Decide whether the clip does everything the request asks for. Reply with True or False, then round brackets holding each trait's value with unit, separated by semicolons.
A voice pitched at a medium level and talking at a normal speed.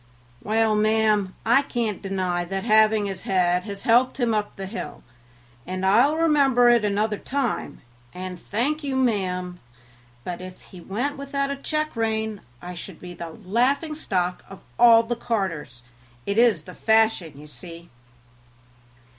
False (215 Hz; 155 wpm)